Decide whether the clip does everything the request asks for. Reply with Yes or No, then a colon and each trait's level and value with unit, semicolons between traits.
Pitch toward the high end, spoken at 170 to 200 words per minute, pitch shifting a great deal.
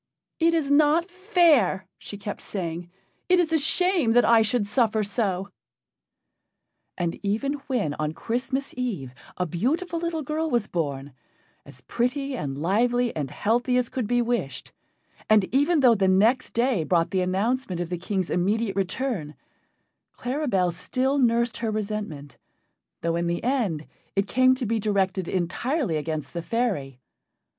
No: high, 225 Hz; average, 150 wpm; wide, 6.4 semitones